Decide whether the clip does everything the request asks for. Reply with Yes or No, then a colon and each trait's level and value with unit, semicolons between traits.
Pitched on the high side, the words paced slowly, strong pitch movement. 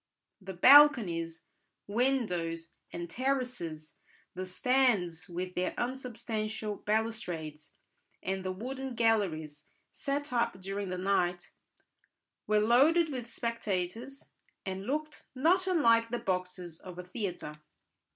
Yes: high, 210 Hz; slow, 110 wpm; wide, 5.9 semitones